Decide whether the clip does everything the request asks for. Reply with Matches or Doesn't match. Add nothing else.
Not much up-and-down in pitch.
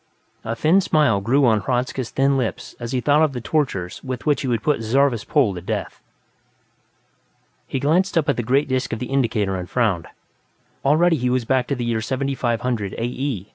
Doesn't match